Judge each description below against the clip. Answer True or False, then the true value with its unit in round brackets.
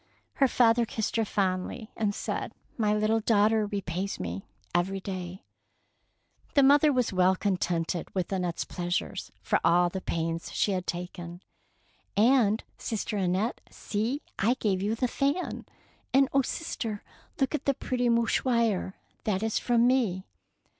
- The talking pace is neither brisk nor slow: True (155 wpm)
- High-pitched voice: True (210 Hz)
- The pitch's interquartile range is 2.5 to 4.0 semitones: False (4.4 semitones)